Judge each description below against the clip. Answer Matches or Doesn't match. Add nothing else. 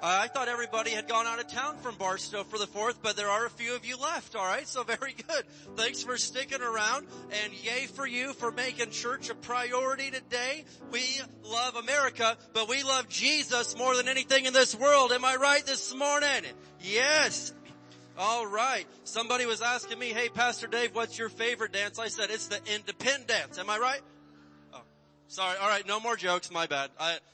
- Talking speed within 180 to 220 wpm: Matches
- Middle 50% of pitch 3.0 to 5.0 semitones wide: Matches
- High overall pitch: Matches